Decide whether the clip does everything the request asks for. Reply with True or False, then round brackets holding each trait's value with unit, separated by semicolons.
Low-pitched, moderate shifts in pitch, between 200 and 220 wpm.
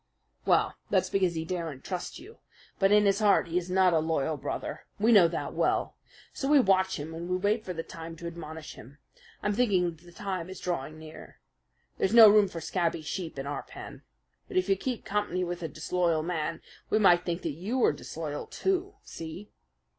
False (180 Hz; 3.7 semitones; 205 wpm)